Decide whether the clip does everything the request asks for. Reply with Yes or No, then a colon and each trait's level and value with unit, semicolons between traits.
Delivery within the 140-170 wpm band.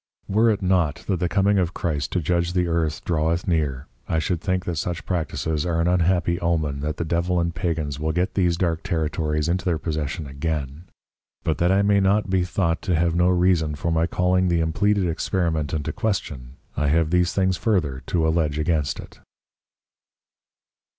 No: average, 190 wpm